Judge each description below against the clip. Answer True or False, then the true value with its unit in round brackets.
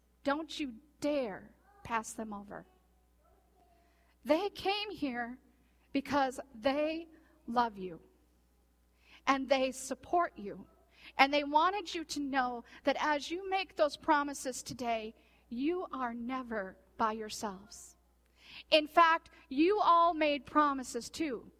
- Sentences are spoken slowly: True (115 wpm)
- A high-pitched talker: True (275 Hz)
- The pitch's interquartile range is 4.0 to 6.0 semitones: True (5.4 semitones)